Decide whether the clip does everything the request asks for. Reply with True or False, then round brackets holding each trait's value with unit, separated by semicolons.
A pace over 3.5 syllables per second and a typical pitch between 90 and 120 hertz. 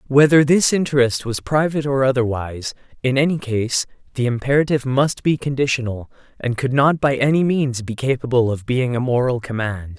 False (5.5 syllables/s; 130 Hz)